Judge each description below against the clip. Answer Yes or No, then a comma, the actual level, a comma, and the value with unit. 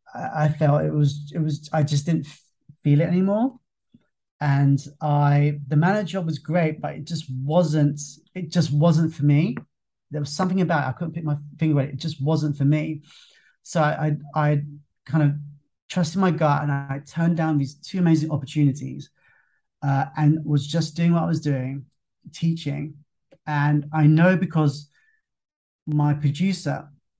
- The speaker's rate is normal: Yes, average, 170 wpm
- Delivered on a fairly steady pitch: Yes, narrow, 2.1 semitones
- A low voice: No, medium, 150 Hz